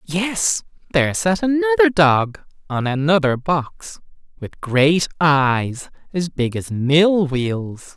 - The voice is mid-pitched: Yes, medium, 160 Hz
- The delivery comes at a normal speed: No, slow, 120 wpm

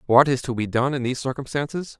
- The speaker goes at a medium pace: No, fast, 240 wpm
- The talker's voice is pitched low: Yes, low, 130 Hz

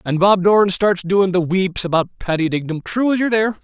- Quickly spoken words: Yes, fast, 230 wpm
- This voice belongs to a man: Yes, male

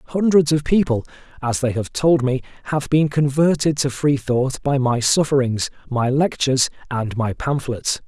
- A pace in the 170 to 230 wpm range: No, average, 155 wpm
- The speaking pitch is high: No, low, 135 Hz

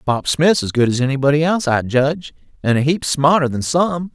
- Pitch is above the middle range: No, medium, 145 Hz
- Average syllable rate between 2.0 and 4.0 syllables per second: No, 5.6 syllables/s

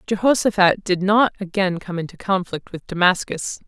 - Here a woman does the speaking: Yes, female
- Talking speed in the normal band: Yes, average, 145 wpm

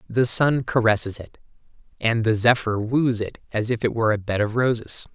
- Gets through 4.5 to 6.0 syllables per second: Yes, 5.5 syllables/s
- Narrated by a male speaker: Yes, male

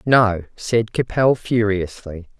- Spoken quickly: No, slow, 100 wpm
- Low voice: Yes, low, 105 Hz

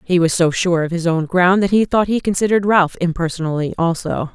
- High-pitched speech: No, medium, 180 Hz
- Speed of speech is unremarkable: No, fast, 220 wpm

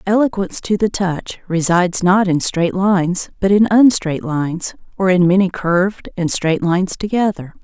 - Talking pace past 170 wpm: No, average, 165 wpm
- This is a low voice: No, medium, 185 Hz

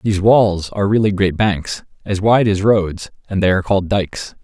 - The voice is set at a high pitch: No, low, 100 Hz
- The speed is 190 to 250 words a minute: Yes, fast, 205 wpm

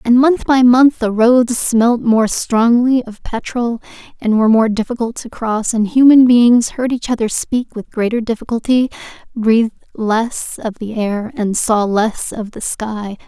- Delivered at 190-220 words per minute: No, average, 170 wpm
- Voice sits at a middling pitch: No, high, 230 Hz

